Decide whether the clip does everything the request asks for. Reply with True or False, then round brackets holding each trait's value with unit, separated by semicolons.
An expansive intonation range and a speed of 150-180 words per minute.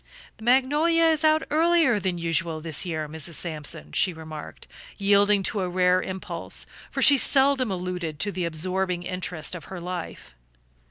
True (6.1 semitones; 160 wpm)